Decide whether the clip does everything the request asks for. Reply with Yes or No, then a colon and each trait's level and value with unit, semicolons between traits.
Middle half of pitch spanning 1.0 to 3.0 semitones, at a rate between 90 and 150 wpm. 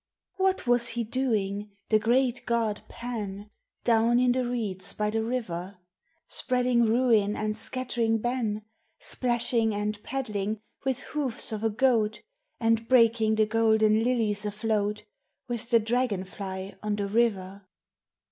Yes: narrow, 2.4 semitones; slow, 135 wpm